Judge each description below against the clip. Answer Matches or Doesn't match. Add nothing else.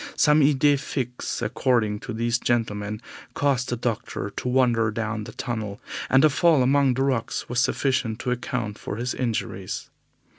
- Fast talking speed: Doesn't match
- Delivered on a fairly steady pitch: Doesn't match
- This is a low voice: Matches